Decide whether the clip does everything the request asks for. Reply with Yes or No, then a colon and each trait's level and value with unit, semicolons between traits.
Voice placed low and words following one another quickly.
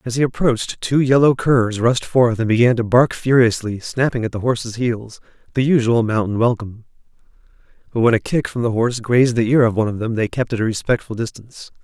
Yes: low, 120 Hz; fast, 215 wpm